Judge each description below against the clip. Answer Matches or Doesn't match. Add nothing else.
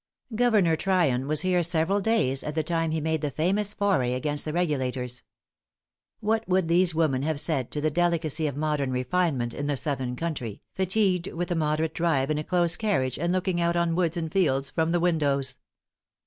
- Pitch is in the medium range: Matches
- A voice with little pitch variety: Doesn't match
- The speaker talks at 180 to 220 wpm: Matches